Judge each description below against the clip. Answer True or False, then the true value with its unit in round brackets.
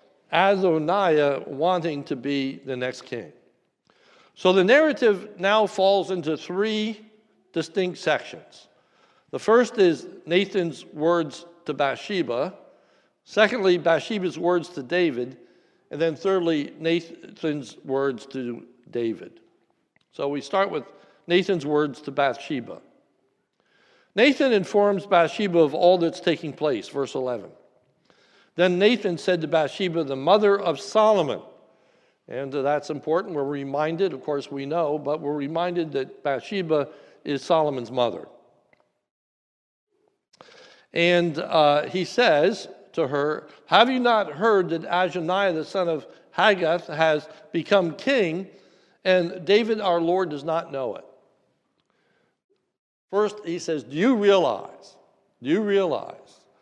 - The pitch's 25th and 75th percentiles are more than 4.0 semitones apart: True (4.9 semitones)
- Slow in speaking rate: True (120 wpm)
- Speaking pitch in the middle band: True (170 Hz)